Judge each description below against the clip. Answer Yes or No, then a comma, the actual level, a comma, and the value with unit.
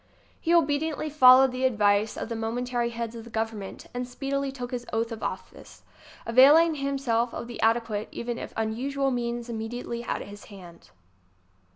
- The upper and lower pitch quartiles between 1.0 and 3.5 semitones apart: Yes, average, 3.1 semitones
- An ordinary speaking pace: Yes, average, 170 wpm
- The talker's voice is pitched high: Yes, high, 240 Hz